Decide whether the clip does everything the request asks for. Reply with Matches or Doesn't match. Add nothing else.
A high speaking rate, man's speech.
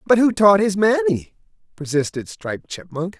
Doesn't match